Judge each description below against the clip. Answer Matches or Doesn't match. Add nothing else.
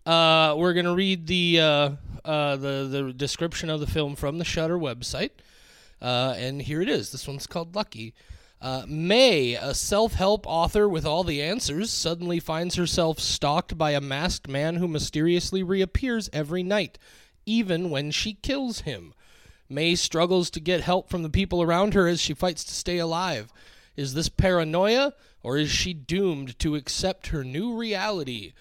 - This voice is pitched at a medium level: Matches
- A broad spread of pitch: Doesn't match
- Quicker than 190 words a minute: Doesn't match